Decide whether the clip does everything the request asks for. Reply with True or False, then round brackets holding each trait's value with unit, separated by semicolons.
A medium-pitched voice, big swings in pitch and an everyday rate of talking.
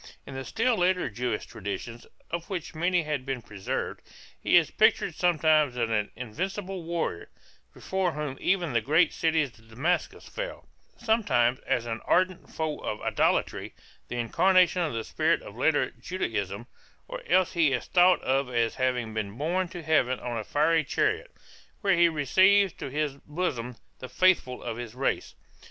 True (150 Hz; 6.7 semitones; 165 wpm)